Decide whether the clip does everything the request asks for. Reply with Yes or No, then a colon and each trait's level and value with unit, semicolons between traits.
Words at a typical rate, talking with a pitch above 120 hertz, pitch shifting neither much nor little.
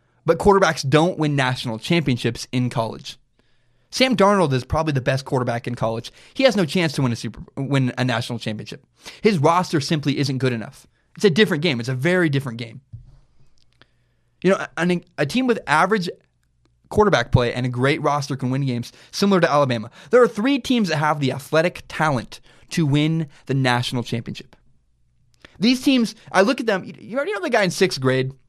No: average, 190 wpm; medium, 140 Hz; wide, 6.4 semitones